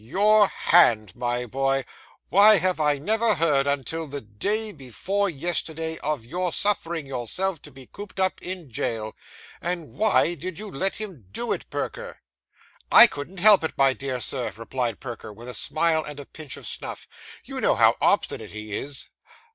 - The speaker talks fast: No, average, 170 wpm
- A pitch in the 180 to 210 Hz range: No, medium, 155 Hz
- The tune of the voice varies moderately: No, wide, 6.4 semitones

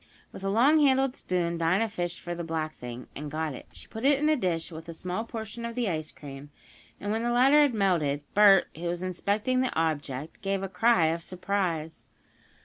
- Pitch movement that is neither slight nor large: No, wide, 5.8 semitones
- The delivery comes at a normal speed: No, fast, 210 wpm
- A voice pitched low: No, medium, 185 Hz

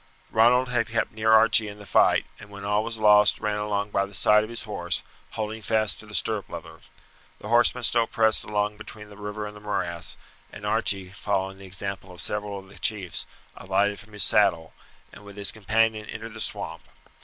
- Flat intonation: Yes, narrow, 1.6 semitones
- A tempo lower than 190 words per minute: No, fast, 205 wpm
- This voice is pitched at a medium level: No, low, 105 Hz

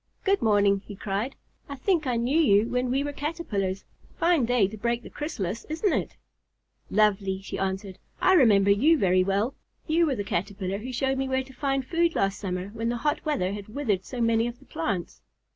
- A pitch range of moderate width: No, wide, 5.8 semitones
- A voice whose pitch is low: No, high, 235 Hz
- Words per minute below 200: No, fast, 205 wpm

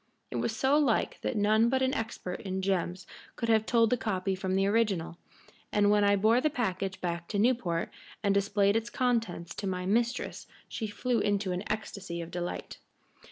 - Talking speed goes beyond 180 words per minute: Yes, average, 190 wpm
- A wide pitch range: No, average, 3.5 semitones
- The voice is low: No, high, 205 Hz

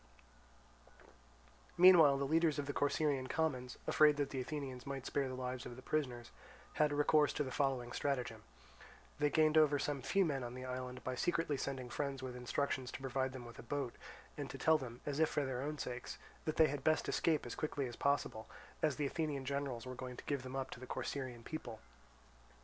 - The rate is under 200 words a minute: No, fast, 205 wpm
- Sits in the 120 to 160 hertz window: Yes, low, 135 Hz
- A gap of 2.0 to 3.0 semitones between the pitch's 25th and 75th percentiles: Yes, narrow, 2.6 semitones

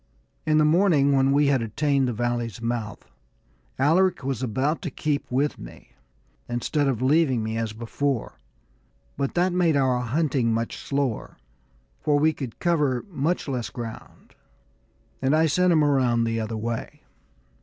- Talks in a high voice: No, low, 135 Hz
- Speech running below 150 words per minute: No, average, 155 wpm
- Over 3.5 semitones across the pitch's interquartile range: Yes, average, 4.3 semitones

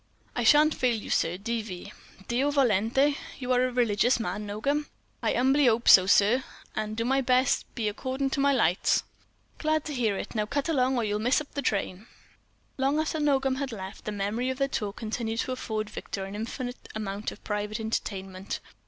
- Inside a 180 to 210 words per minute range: Yes, average, 195 wpm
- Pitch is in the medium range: No, high, 235 Hz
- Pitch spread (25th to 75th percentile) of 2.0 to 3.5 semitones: No, average, 4.2 semitones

